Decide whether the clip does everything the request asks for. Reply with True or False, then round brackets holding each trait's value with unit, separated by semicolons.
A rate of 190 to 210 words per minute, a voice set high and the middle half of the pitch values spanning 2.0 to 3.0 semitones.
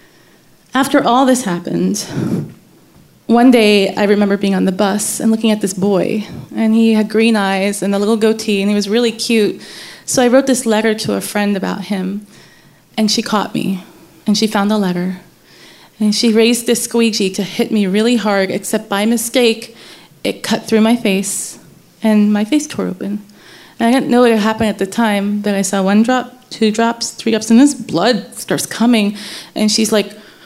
True (195 wpm; 215 Hz; 2.5 semitones)